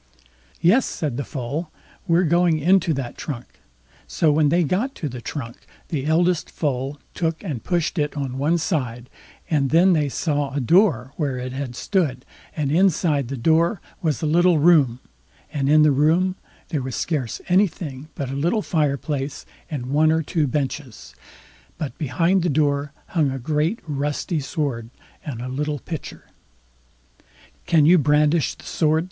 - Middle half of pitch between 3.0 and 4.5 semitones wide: Yes, average, 3.5 semitones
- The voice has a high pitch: No, medium, 150 Hz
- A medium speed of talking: Yes, average, 165 wpm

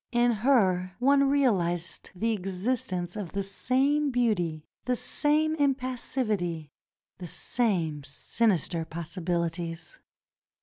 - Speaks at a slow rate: Yes, slow, 95 wpm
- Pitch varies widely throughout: Yes, wide, 6.6 semitones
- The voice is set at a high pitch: Yes, high, 200 Hz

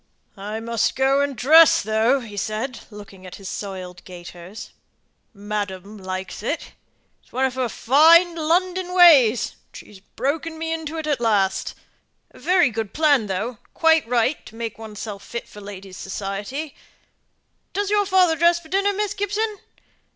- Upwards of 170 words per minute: No, average, 160 wpm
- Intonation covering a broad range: Yes, wide, 7.9 semitones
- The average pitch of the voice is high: Yes, high, 245 Hz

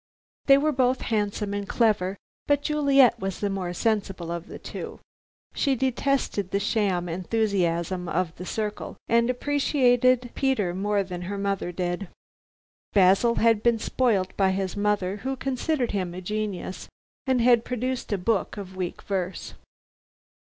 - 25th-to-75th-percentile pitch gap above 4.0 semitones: Yes, average, 4.7 semitones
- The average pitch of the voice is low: No, high, 205 Hz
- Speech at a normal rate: Yes, average, 150 wpm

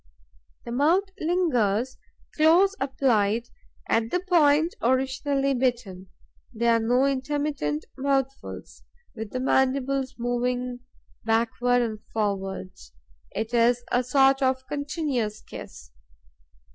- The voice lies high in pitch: Yes, very high, 255 Hz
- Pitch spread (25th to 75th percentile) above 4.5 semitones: No, average, 3.3 semitones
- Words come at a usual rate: No, slow, 105 wpm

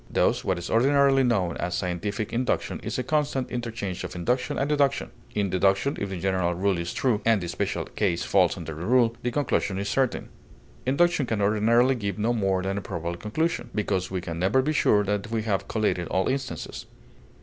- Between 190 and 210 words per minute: Yes, average, 200 wpm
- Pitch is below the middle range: Yes, low, 105 Hz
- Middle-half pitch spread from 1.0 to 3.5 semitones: No, average, 4.9 semitones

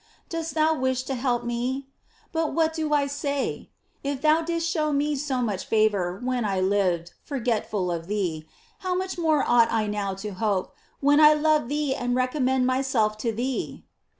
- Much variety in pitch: Yes, wide, 5.9 semitones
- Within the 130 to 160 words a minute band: No, average, 180 wpm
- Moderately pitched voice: No, very high, 255 Hz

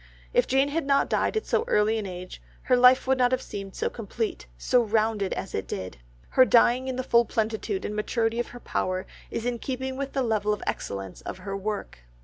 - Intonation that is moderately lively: Yes, average, 4.2 semitones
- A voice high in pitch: Yes, high, 225 Hz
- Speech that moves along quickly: Yes, fast, 210 wpm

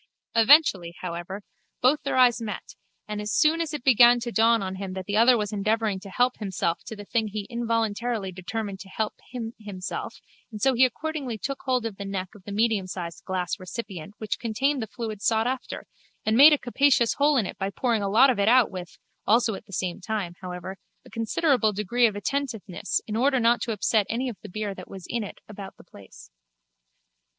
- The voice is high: Yes, high, 220 Hz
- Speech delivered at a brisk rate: Yes, fast, 210 wpm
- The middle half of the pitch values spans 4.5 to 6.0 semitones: No, average, 3.7 semitones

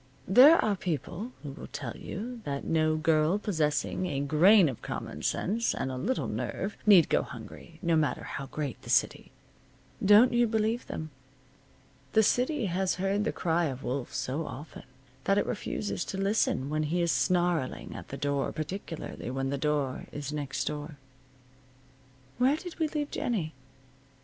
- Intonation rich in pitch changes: Yes, wide, 6.3 semitones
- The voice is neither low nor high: Yes, medium, 165 Hz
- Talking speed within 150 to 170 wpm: Yes, average, 165 wpm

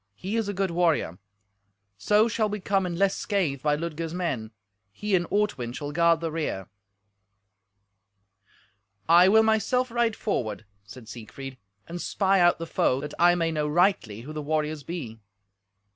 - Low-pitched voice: No, medium, 170 Hz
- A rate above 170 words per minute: No, average, 160 wpm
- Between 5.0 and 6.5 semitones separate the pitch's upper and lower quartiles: Yes, average, 5.3 semitones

